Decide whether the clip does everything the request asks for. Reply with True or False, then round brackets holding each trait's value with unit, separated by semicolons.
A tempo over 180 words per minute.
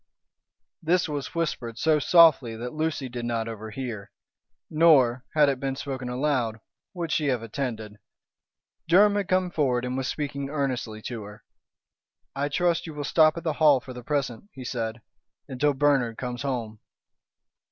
False (160 wpm)